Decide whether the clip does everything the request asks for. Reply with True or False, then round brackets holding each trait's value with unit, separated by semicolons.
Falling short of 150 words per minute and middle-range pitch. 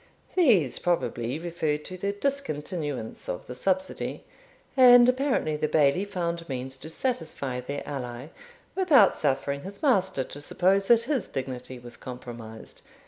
True (140 wpm; 160 Hz)